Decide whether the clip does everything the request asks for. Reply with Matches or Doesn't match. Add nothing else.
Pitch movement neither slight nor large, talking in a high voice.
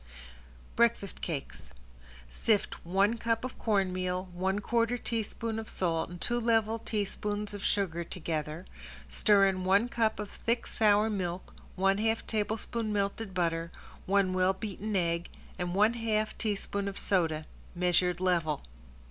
Matches